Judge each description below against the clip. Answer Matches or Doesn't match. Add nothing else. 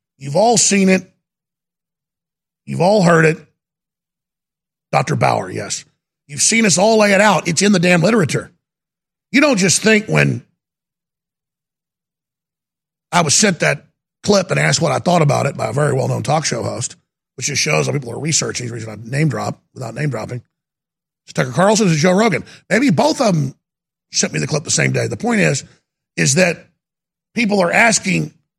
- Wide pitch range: Doesn't match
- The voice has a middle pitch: Matches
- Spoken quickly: Doesn't match